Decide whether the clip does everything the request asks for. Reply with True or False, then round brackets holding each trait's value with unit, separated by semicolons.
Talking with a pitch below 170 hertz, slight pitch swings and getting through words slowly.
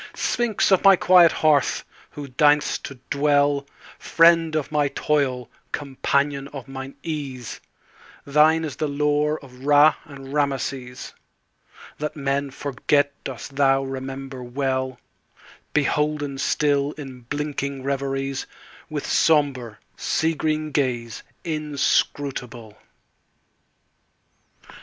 True (140 Hz; 1.9 semitones; 90 wpm)